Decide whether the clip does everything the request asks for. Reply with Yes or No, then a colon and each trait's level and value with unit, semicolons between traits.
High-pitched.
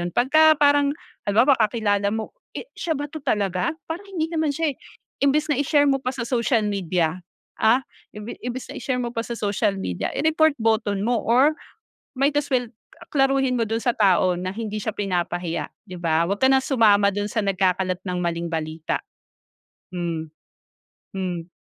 Yes: high, 225 Hz